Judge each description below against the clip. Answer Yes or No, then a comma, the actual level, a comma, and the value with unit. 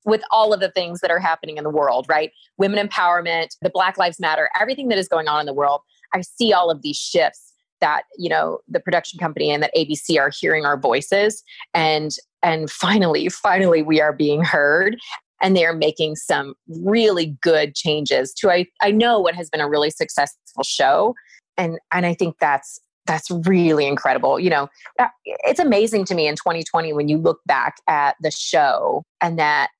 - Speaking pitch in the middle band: Yes, medium, 165 Hz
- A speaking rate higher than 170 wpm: Yes, average, 195 wpm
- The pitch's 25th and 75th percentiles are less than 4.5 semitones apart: Yes, average, 3.7 semitones